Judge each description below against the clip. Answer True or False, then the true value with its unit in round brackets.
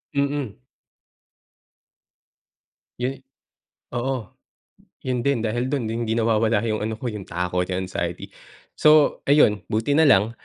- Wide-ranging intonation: False (4.0 semitones)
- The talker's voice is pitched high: False (115 Hz)